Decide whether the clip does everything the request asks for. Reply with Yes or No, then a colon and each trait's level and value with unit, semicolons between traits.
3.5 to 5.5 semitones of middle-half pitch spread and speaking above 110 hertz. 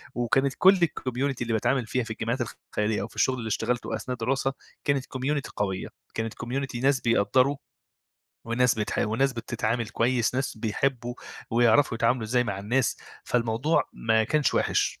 No: average, 2.9 semitones; low, 120 Hz